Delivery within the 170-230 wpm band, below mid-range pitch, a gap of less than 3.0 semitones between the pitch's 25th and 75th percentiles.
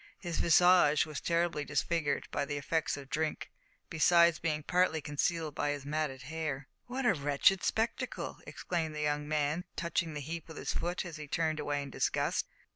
No: average, 180 wpm; medium, 155 Hz; narrow, 2.6 semitones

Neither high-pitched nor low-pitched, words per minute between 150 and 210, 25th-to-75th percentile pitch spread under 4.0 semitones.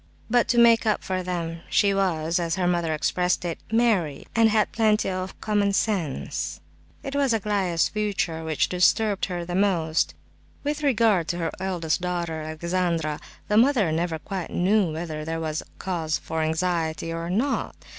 No: medium, 180 Hz; average, 160 wpm; average, 4.3 semitones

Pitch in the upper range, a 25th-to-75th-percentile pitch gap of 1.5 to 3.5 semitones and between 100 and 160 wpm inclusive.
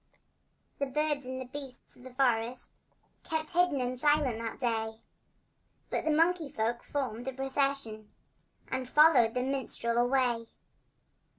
Yes: very high, 260 Hz; average, 3.2 semitones; slow, 135 wpm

